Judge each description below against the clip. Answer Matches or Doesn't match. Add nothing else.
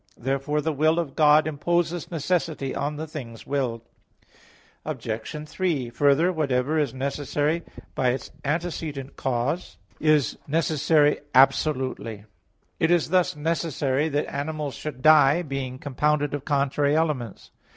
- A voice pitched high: Doesn't match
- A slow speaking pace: Matches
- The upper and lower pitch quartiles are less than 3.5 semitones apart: Matches